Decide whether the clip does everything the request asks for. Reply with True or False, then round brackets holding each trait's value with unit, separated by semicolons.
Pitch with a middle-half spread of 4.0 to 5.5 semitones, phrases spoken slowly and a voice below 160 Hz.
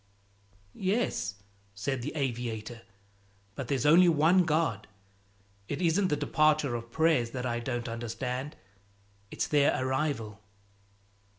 True (4.7 semitones; 115 wpm; 135 Hz)